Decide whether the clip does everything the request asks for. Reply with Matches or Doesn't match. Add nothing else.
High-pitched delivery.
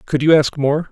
Doesn't match